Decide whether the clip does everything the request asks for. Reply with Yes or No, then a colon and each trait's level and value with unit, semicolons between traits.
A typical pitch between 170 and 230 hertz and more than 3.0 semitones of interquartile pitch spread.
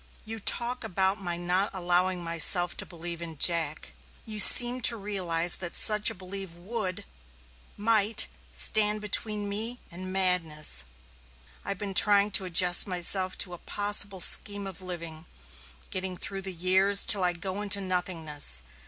No: high, 190 Hz; average, 2.7 semitones